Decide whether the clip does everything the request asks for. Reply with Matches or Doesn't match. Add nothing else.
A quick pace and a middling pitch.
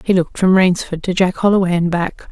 Matches